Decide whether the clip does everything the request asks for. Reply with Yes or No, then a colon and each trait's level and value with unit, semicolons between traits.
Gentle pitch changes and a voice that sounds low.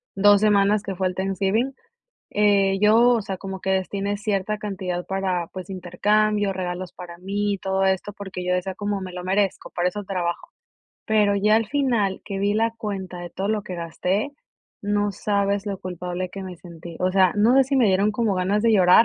No: narrow, 2.1 semitones; high, 195 Hz